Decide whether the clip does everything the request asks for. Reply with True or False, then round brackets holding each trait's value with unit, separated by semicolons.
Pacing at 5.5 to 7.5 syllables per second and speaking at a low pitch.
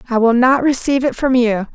False (6.0 syllables/s; 250 Hz)